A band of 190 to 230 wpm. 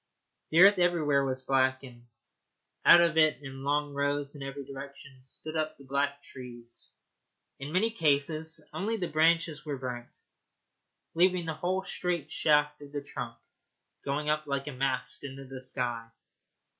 No: average, 155 wpm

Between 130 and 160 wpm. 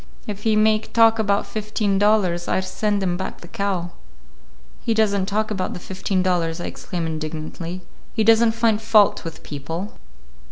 No: average, 175 wpm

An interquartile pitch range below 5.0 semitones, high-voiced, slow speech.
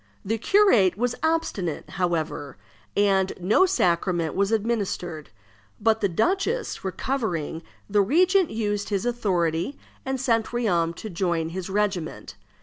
No: wide, 5.6 semitones; high, 200 Hz; slow, 125 wpm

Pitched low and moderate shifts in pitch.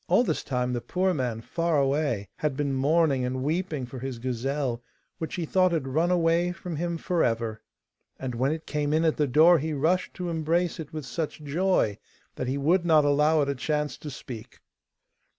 No: medium, 150 Hz; average, 4.1 semitones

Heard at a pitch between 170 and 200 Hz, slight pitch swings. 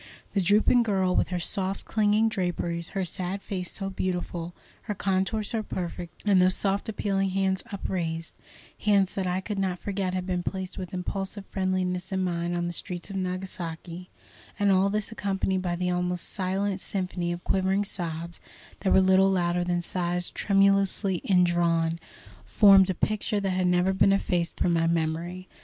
Yes: medium, 185 Hz; narrow, 1.8 semitones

